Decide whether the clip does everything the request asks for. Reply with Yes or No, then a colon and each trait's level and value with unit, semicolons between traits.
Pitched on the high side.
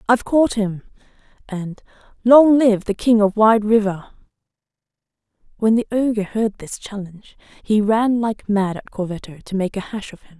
Yes: high, 210 Hz